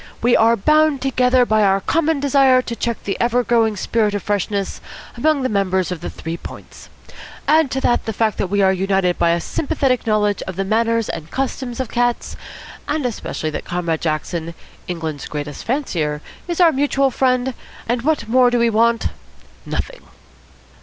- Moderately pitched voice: No, high, 230 Hz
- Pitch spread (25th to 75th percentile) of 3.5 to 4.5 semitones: No, average, 5.3 semitones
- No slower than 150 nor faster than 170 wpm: No, average, 180 wpm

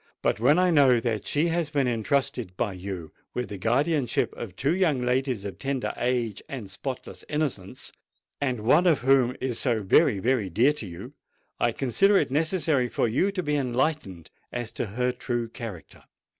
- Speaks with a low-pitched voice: Yes, low, 125 Hz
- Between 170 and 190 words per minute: Yes, average, 180 wpm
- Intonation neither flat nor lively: Yes, average, 4.5 semitones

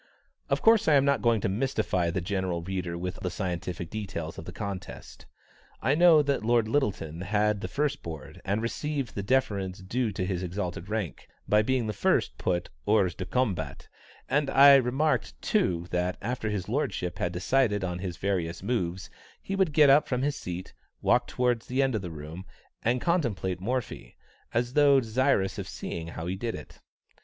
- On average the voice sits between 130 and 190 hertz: No, low, 105 Hz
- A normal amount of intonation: No, wide, 6.3 semitones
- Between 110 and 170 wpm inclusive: No, average, 185 wpm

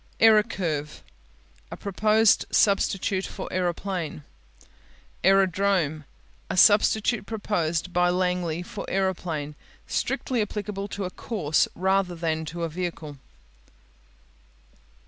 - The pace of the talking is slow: Yes, slow, 95 wpm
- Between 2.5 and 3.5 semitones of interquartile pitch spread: Yes, average, 3.2 semitones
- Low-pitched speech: No, medium, 185 Hz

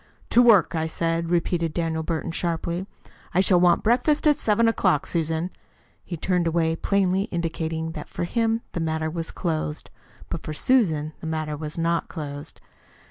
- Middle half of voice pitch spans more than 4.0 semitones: No, narrow, 2.6 semitones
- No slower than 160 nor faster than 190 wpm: Yes, average, 165 wpm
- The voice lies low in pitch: No, medium, 170 Hz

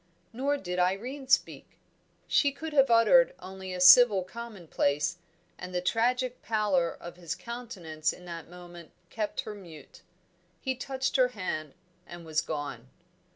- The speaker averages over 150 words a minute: No, average, 145 wpm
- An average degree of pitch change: No, wide, 6.2 semitones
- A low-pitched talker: No, high, 190 Hz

